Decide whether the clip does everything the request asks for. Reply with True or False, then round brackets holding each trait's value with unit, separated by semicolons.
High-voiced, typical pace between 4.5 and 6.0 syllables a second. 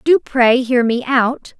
False (255 Hz; 3.4 syllables/s)